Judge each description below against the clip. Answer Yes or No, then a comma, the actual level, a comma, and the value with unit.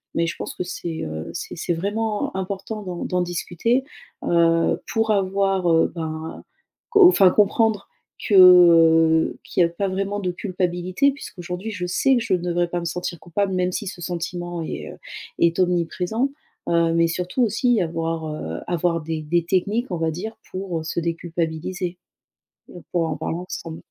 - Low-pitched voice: No, medium, 175 Hz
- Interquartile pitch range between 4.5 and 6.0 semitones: No, average, 2.8 semitones